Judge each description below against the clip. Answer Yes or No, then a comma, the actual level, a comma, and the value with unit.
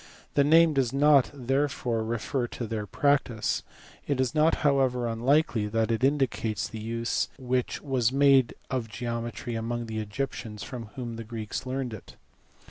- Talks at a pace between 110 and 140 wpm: No, average, 155 wpm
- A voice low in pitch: Yes, low, 120 Hz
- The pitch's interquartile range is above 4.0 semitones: No, average, 3.2 semitones